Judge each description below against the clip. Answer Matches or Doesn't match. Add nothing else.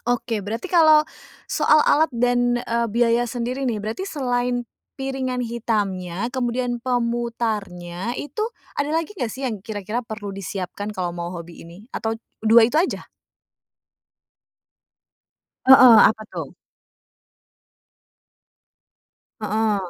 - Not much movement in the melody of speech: Doesn't match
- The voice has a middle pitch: Doesn't match